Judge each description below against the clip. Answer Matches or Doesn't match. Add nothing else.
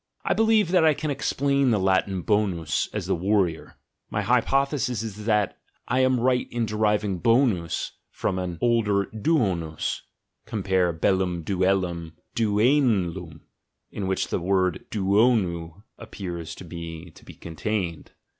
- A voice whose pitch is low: Matches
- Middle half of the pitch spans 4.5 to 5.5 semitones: Matches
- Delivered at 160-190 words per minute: Doesn't match